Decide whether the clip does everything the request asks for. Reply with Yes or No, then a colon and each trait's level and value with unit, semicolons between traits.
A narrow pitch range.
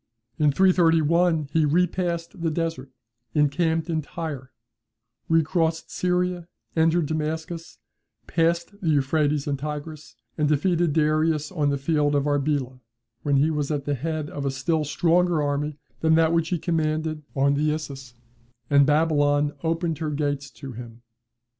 Yes: narrow, 2.2 semitones